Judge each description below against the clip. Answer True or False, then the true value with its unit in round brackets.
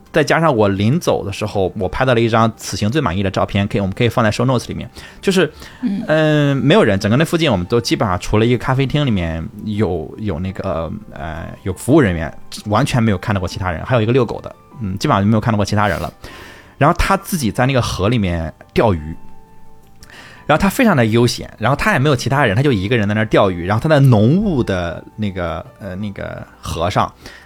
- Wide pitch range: False (5.0 semitones)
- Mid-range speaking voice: False (110 Hz)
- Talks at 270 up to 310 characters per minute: False (355 characters per minute)